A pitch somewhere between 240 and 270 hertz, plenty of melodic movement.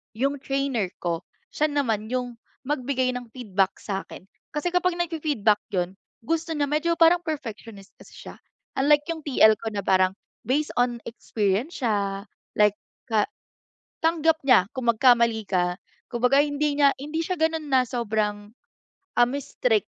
Yes: very high, 250 Hz; wide, 5.9 semitones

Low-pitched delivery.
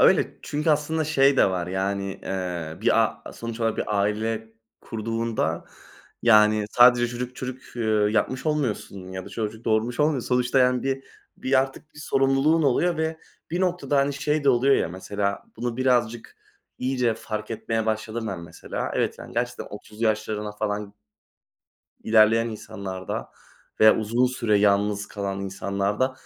Yes: low, 115 Hz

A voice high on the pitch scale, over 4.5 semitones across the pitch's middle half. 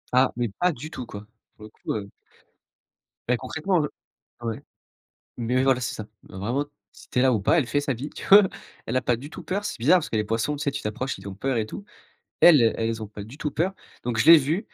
No: low, 130 Hz; average, 4.9 semitones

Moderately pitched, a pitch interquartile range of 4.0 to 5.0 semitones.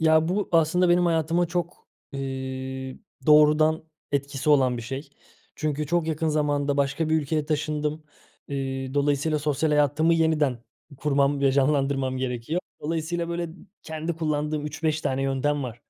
No: medium, 150 Hz; narrow, 2.6 semitones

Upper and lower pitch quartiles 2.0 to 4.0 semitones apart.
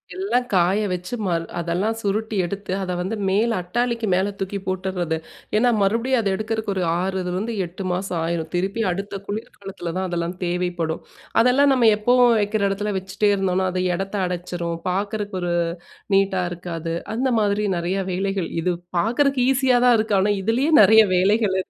Yes: average, 3.4 semitones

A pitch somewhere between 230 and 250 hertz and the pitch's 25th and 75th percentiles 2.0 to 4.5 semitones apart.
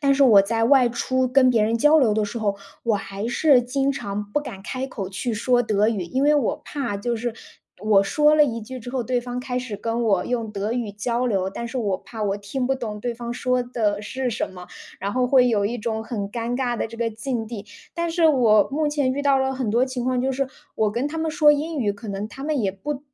Yes: high, 240 Hz; average, 3.8 semitones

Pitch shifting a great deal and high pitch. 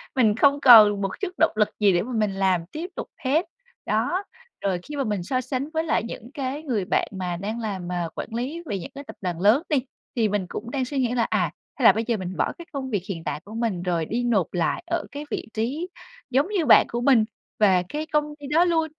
Yes: wide, 6.3 semitones; high, 235 Hz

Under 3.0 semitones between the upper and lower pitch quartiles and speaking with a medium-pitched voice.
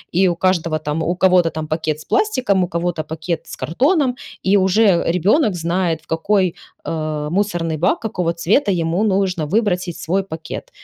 No: average, 3.3 semitones; medium, 175 Hz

